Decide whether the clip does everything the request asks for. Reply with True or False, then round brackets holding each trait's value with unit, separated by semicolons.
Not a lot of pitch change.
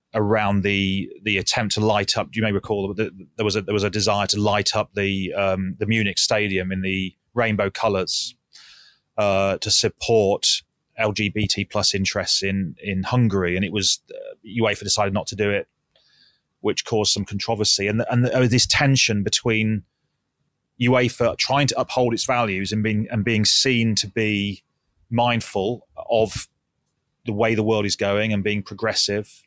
True (2.2 semitones)